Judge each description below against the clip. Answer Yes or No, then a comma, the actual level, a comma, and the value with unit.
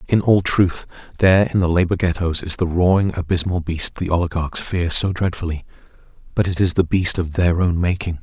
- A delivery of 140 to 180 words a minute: No, average, 190 wpm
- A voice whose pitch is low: Yes, very low, 85 Hz